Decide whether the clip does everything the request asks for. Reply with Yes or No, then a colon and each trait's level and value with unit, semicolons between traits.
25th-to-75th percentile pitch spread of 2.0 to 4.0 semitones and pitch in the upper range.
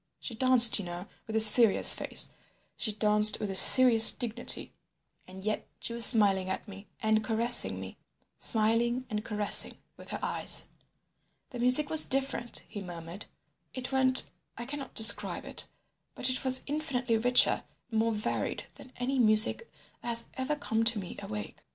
Yes: average, 3.2 semitones; high, 230 Hz